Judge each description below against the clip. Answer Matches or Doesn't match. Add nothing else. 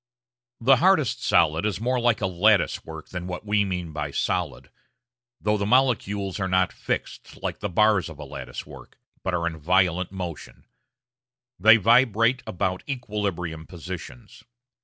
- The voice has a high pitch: Doesn't match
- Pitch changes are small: Doesn't match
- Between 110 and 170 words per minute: Matches